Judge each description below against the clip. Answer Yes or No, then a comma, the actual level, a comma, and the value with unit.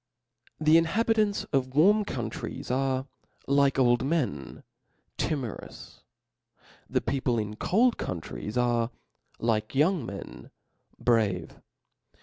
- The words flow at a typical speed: No, slow, 105 wpm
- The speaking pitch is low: Yes, low, 130 Hz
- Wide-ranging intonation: Yes, wide, 5.7 semitones